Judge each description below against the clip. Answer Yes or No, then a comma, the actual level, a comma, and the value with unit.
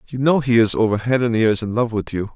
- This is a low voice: Yes, low, 115 Hz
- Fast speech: Yes, fast, 305 wpm